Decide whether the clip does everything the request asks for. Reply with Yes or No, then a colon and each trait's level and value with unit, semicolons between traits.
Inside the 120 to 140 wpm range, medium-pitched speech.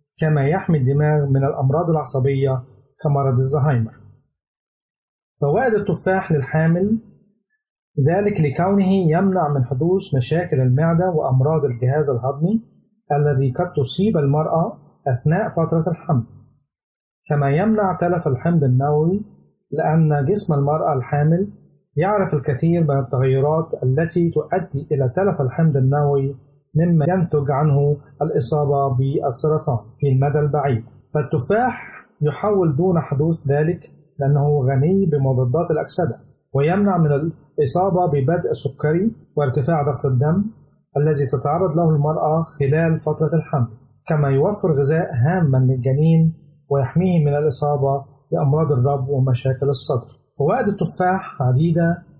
No: average, 110 wpm; medium, 150 Hz